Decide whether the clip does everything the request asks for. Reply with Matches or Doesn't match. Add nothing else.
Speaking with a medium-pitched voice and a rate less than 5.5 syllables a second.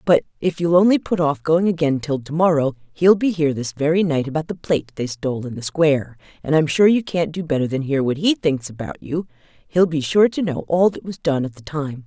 Doesn't match